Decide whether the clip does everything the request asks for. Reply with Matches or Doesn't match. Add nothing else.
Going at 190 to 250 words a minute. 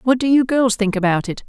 Doesn't match